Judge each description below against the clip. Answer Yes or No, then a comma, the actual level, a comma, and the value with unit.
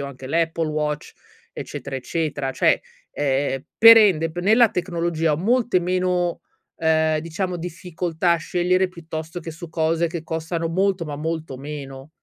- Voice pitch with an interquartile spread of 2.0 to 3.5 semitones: Yes, narrow, 2.5 semitones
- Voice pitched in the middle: Yes, medium, 165 Hz